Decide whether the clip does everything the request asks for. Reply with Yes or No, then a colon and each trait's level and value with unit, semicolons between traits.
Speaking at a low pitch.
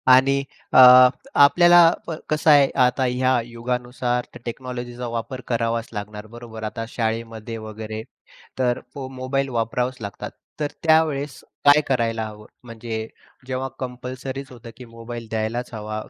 Yes: low, 125 Hz